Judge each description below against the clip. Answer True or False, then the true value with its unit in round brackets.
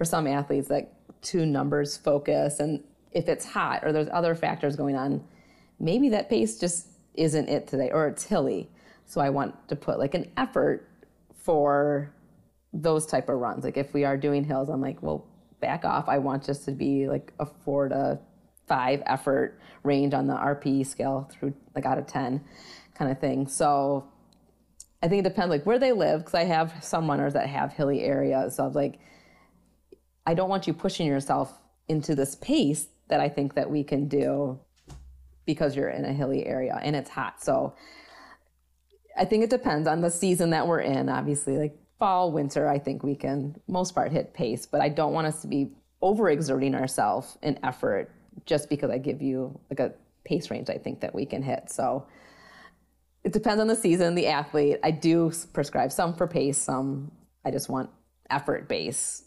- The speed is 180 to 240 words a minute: True (195 wpm)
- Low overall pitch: False (145 Hz)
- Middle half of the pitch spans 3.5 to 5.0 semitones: False (3.1 semitones)